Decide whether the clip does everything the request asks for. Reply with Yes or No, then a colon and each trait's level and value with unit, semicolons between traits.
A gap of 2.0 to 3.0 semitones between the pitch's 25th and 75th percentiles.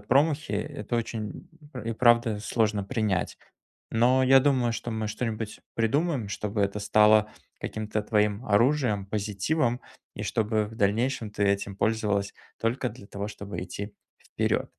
Yes: narrow, 2.6 semitones